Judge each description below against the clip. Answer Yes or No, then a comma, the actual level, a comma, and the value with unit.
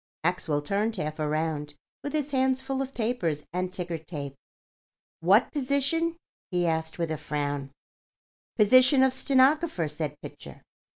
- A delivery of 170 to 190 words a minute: No, slow, 135 wpm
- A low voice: No, medium, 185 Hz